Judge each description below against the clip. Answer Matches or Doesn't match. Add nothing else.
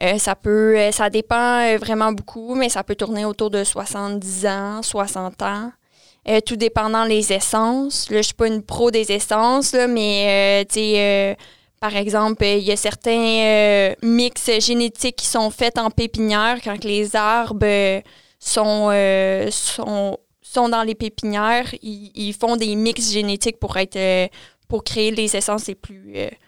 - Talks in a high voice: Matches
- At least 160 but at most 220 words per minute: Matches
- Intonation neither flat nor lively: Doesn't match